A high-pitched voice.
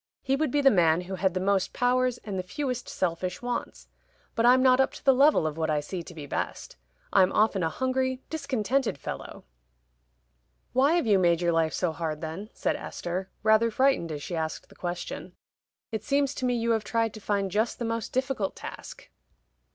Yes: high, 215 Hz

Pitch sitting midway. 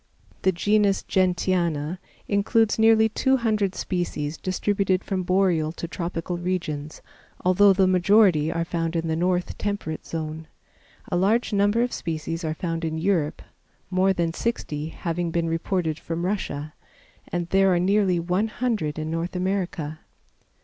Yes: medium, 180 Hz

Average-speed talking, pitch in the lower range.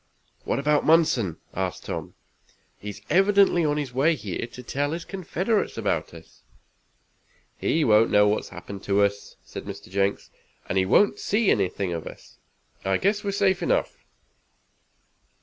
Yes: average, 160 wpm; low, 130 Hz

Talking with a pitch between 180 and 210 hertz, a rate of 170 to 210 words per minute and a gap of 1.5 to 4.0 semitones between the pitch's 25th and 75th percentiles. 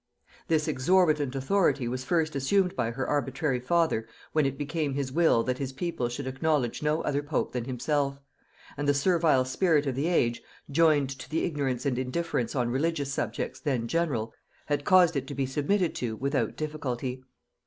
No: medium, 140 Hz; average, 175 wpm; average, 3.6 semitones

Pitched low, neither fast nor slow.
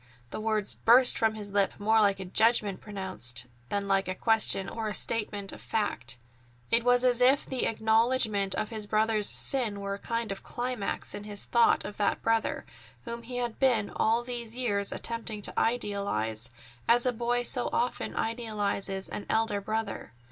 No: high, 220 Hz; average, 175 wpm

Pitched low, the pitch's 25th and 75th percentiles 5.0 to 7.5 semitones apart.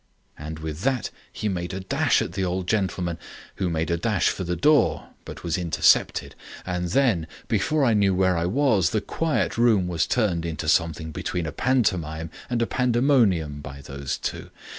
Yes: very low, 90 Hz; wide, 5.4 semitones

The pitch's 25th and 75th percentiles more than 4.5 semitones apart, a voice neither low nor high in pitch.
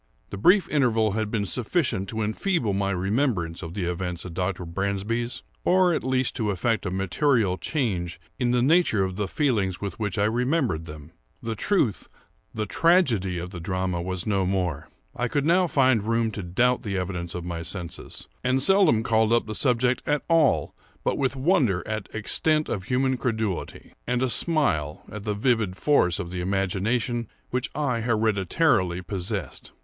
No: wide, 5.4 semitones; low, 110 Hz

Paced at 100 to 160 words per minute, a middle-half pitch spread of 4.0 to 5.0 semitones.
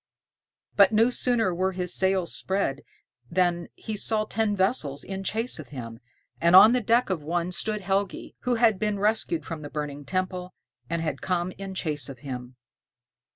No: average, 175 wpm; average, 4.6 semitones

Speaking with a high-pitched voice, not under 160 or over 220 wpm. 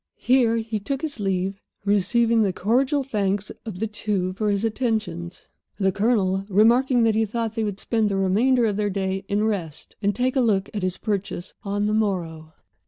Yes: high, 210 Hz; average, 190 wpm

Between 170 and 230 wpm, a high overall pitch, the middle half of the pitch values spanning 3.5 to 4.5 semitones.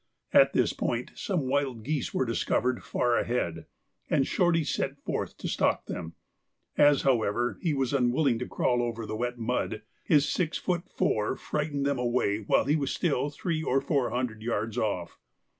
No: average, 175 wpm; low, 125 Hz; average, 4.0 semitones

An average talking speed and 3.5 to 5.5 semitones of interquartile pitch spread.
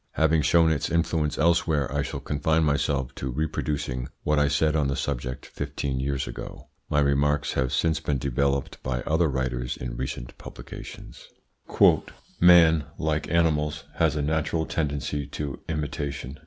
No: average, 150 wpm; narrow, 2.5 semitones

